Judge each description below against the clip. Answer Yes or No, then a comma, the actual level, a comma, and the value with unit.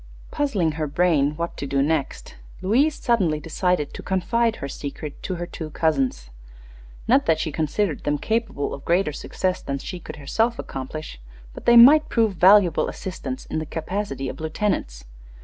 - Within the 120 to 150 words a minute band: No, average, 170 wpm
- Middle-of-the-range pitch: Yes, medium, 165 Hz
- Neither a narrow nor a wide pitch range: No, wide, 6.1 semitones